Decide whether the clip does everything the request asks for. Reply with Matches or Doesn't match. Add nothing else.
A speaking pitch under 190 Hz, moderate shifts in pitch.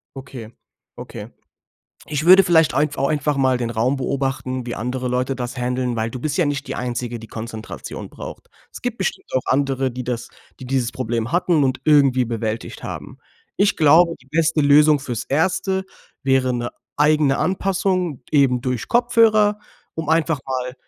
Matches